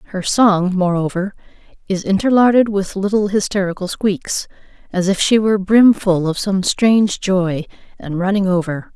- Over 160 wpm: No, average, 145 wpm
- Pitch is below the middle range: No, high, 195 Hz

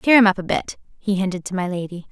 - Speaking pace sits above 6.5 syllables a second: Yes, 6.7 syllables/s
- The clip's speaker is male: No, female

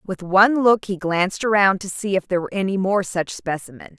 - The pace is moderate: No, fast, 225 wpm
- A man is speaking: No, female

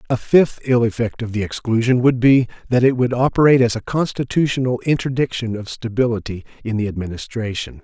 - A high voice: No, low, 120 Hz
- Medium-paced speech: Yes, average, 170 wpm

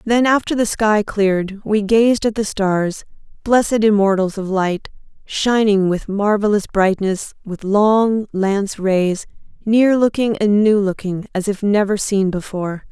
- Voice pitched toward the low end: No, high, 205 Hz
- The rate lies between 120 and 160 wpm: Yes, average, 150 wpm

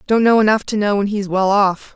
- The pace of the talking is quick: Yes, fast, 275 wpm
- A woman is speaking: Yes, female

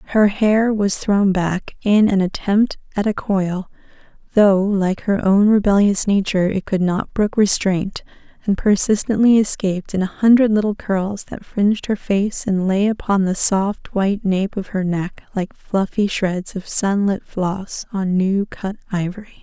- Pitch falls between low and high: No, high, 200 Hz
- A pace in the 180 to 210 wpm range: No, average, 170 wpm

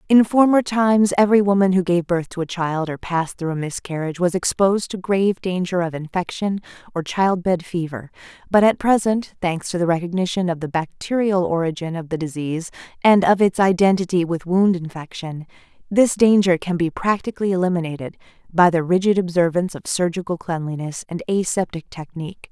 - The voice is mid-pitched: Yes, medium, 180 Hz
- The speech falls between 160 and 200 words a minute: Yes, average, 165 wpm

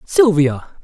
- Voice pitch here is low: No, very high, 250 Hz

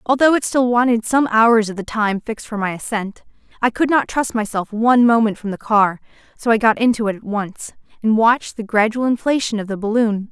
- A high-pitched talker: Yes, high, 225 Hz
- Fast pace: Yes, fast, 220 wpm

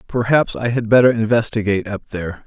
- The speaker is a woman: No, male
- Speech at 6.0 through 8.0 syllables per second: Yes, 6.3 syllables/s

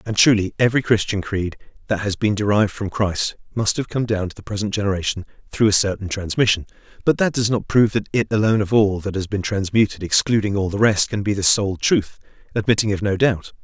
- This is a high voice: No, low, 105 Hz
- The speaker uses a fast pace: Yes, fast, 220 wpm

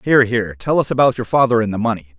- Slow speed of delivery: No, fast, 275 wpm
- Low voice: Yes, low, 115 Hz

